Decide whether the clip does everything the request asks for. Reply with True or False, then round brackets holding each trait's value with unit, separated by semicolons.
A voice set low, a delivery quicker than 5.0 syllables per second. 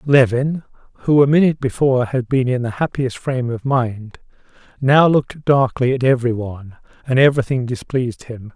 True (130 Hz; 5.5 syllables/s)